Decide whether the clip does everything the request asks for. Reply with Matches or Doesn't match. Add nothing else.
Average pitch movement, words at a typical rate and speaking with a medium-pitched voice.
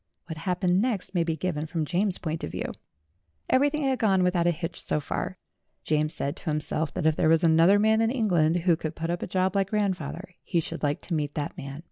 Doesn't match